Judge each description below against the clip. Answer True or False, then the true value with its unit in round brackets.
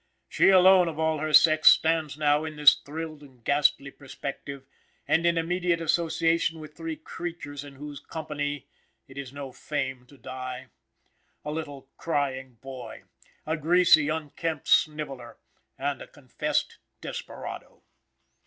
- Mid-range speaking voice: True (150 Hz)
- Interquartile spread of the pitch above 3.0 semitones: False (2.6 semitones)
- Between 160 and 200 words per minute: False (135 wpm)